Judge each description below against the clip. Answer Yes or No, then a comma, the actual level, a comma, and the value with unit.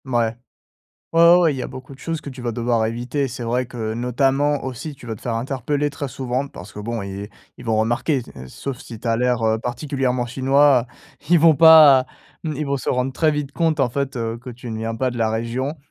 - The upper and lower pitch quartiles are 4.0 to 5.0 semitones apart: No, average, 3.3 semitones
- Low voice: Yes, low, 125 Hz